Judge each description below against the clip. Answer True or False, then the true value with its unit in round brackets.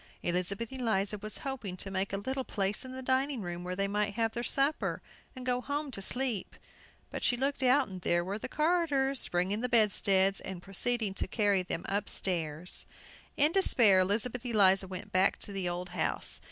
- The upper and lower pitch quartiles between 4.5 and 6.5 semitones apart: True (5.1 semitones)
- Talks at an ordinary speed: True (190 wpm)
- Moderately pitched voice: False (205 Hz)